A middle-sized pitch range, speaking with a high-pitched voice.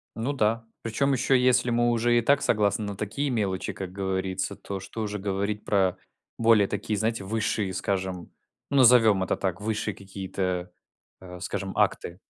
No: average, 3.3 semitones; low, 105 Hz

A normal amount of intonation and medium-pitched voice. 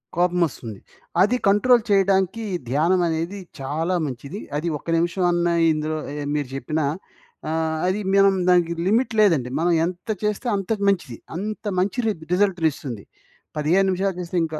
Yes: average, 3.8 semitones; medium, 175 Hz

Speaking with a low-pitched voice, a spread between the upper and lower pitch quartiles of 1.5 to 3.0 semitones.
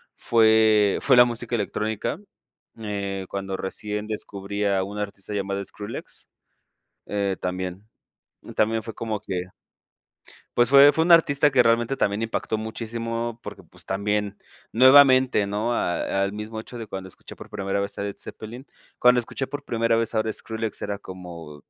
Yes: low, 110 Hz; average, 2.7 semitones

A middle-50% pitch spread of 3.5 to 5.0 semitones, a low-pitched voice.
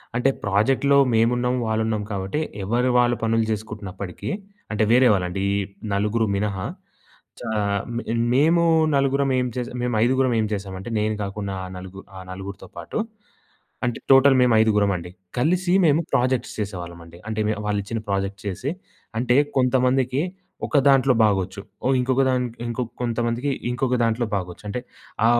Yes: average, 4.2 semitones; low, 115 Hz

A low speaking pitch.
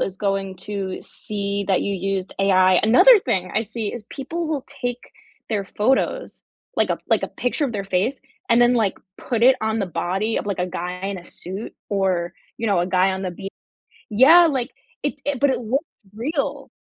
No: high, 210 Hz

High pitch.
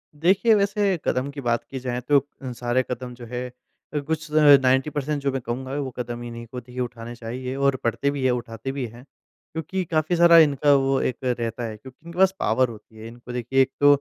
No: low, 130 Hz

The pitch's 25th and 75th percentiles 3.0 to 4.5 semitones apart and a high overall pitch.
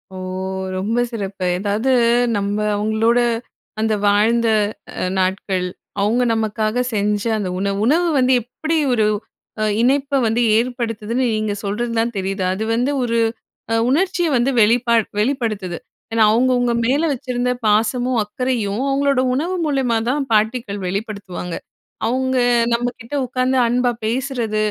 Yes: average, 3.4 semitones; high, 230 Hz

